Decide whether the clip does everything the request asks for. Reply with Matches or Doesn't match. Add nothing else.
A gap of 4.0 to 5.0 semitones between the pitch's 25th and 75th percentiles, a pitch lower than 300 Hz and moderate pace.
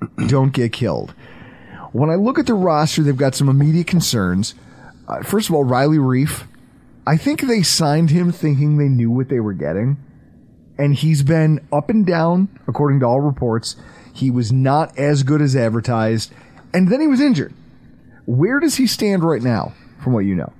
Matches